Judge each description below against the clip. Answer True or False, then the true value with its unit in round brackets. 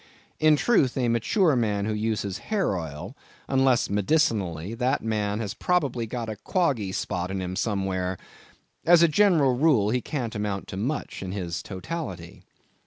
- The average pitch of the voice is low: True (110 Hz)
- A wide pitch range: True (6.2 semitones)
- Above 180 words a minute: False (160 wpm)